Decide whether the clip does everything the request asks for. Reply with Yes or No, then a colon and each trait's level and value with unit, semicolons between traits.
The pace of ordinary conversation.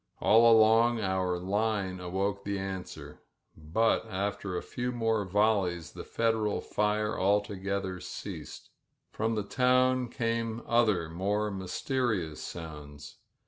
No: slow, 120 wpm